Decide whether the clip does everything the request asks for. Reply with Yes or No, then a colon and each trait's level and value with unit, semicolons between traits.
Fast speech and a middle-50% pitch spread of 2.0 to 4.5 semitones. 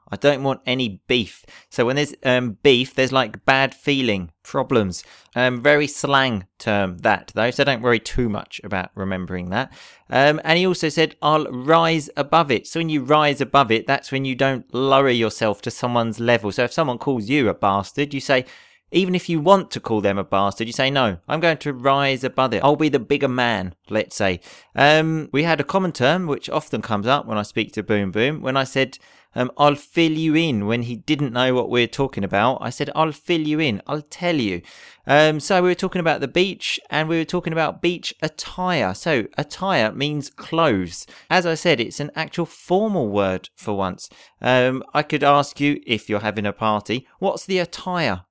No: fast, 210 wpm; wide, 5.4 semitones